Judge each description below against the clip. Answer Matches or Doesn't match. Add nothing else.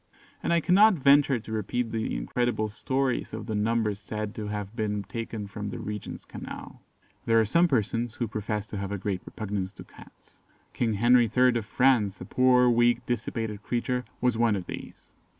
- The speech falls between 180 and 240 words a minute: Matches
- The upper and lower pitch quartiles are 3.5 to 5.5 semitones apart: Doesn't match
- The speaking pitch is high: Doesn't match